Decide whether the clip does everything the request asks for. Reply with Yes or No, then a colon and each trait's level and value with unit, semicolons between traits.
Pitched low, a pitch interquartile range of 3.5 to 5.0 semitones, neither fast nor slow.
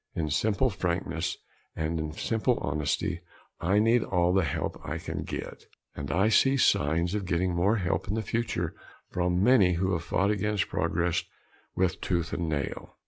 Yes: very low, 90 Hz; average, 3.8 semitones; average, 170 wpm